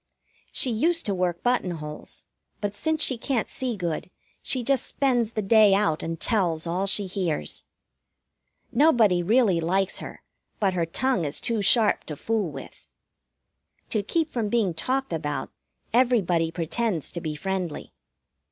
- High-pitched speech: Yes, high, 200 Hz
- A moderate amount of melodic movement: No, wide, 5.8 semitones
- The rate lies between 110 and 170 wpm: Yes, average, 150 wpm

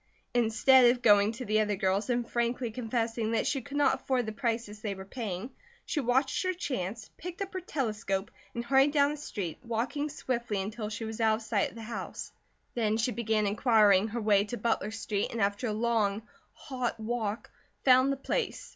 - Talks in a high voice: Yes, high, 230 Hz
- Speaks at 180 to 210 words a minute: Yes, average, 200 wpm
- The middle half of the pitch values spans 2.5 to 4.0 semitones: Yes, average, 3.1 semitones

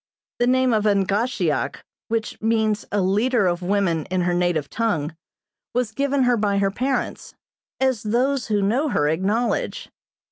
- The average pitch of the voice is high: Yes, high, 215 Hz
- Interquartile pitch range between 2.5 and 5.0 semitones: Yes, average, 4.5 semitones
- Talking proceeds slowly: No, average, 150 wpm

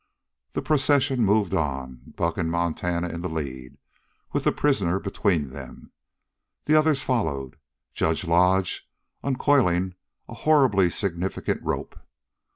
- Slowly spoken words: Yes, slow, 120 wpm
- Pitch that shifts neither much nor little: No, wide, 7.6 semitones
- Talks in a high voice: No, very low, 90 Hz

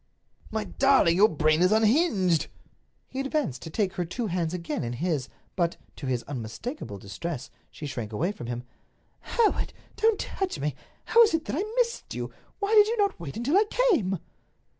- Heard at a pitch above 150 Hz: Yes, medium, 185 Hz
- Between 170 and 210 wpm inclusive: Yes, average, 180 wpm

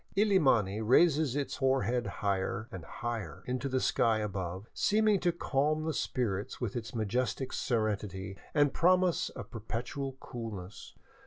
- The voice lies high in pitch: No, low, 120 Hz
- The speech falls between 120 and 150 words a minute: Yes, average, 140 wpm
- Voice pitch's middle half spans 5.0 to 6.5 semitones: Yes, wide, 5.6 semitones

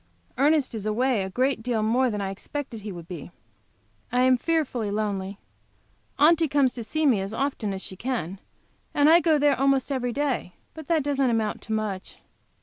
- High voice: Yes, high, 245 Hz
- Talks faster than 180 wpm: Yes, average, 190 wpm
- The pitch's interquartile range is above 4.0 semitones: Yes, average, 5.1 semitones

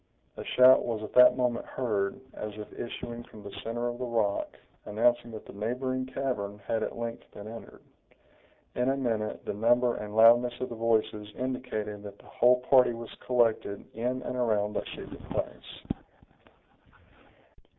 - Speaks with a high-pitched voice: No, low, 115 Hz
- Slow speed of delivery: No, average, 165 wpm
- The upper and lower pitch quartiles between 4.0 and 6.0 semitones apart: No, average, 2.7 semitones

